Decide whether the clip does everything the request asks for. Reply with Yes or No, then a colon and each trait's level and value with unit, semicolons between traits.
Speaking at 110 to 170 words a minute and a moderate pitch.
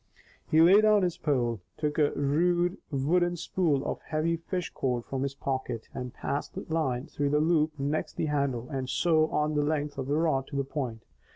No: average, 200 wpm; medium, 150 Hz